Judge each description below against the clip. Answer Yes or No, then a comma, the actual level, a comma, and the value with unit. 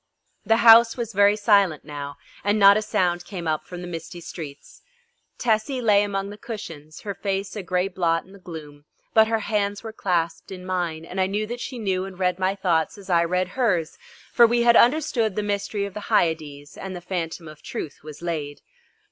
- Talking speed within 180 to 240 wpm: Yes, fast, 205 wpm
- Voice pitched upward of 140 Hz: Yes, high, 190 Hz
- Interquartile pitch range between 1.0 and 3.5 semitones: No, average, 3.9 semitones